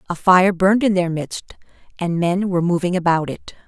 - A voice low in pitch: No, medium, 180 Hz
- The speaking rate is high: No, average, 195 wpm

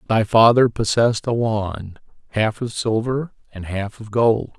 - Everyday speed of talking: Yes, average, 155 wpm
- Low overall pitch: Yes, low, 110 Hz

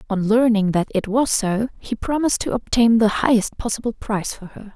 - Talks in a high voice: Yes, high, 220 Hz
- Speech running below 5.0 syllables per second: No, 5.4 syllables/s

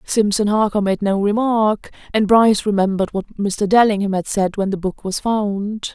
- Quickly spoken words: No, average, 180 wpm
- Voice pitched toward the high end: Yes, high, 205 Hz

